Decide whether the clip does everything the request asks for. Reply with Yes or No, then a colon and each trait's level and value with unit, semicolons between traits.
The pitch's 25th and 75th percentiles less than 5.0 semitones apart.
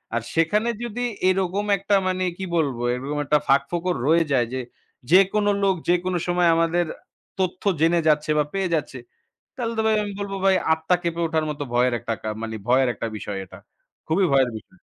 No: wide, 5.5 semitones